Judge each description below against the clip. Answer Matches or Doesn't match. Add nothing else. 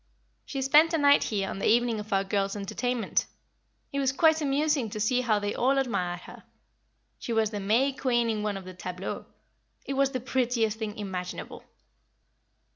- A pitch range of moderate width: Matches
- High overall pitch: Matches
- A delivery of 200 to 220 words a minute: Doesn't match